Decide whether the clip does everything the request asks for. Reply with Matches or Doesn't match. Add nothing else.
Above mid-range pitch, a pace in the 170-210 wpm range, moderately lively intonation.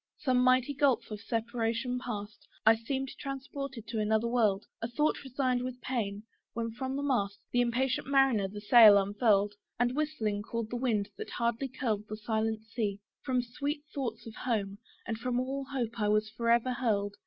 Matches